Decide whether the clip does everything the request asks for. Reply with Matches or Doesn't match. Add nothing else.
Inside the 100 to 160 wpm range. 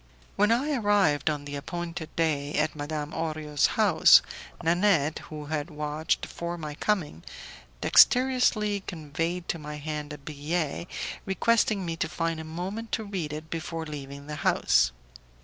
Matches